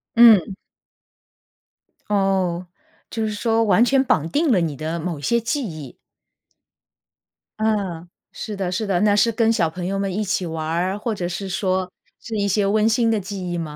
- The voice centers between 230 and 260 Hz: No, high, 195 Hz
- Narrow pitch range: No, average, 3.8 semitones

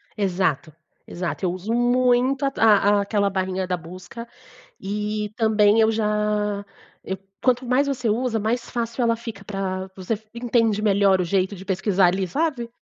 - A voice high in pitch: Yes, high, 210 Hz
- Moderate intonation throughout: Yes, average, 3.6 semitones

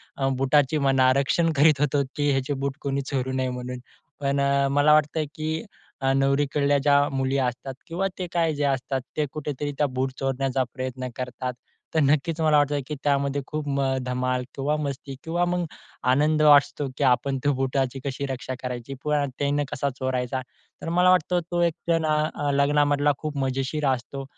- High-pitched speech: No, medium, 140 Hz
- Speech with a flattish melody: Yes, narrow, 2.2 semitones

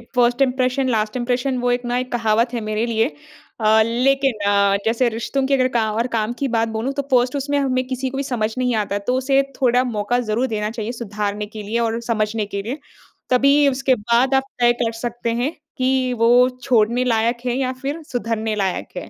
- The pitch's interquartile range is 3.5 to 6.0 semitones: No, narrow, 2.6 semitones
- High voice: Yes, high, 240 Hz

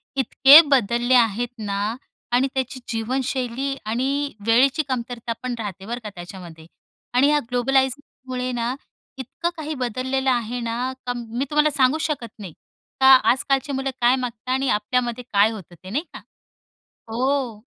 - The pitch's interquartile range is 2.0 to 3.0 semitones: Yes, average, 2.7 semitones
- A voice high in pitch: Yes, very high, 250 Hz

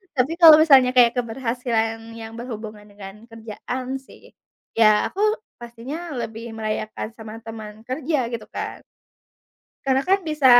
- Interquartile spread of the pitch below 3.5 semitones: Yes, average, 2.8 semitones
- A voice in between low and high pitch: No, high, 235 Hz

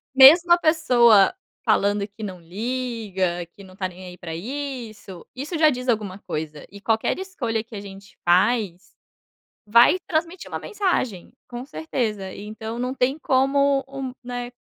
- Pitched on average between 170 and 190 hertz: No, high, 235 Hz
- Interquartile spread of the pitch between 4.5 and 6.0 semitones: Yes, wide, 5.5 semitones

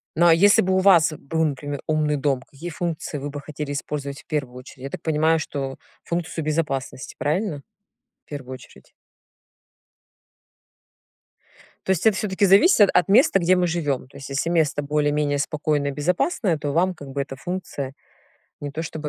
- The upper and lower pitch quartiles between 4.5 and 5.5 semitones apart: No, average, 3.4 semitones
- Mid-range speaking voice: Yes, medium, 150 Hz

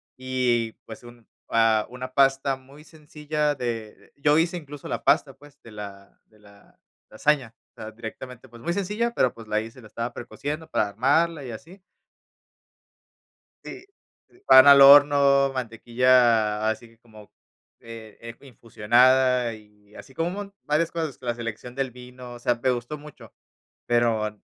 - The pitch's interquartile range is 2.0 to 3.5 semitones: No, average, 4.1 semitones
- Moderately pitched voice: No, low, 125 Hz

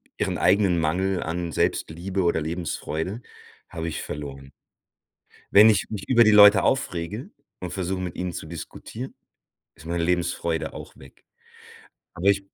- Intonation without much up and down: No, average, 3.3 semitones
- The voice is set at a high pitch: No, very low, 90 Hz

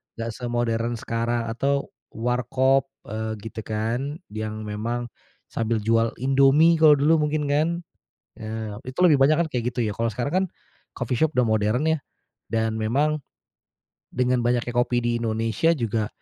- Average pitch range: Yes, average, 3.6 semitones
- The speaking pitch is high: No, low, 120 Hz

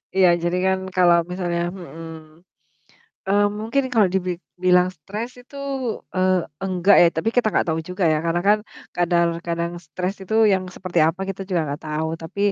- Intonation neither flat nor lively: No, narrow, 2.2 semitones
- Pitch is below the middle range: No, medium, 180 Hz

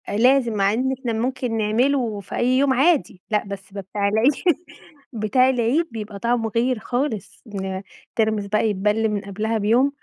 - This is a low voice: No, high, 220 Hz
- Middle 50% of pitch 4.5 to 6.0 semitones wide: No, average, 3.4 semitones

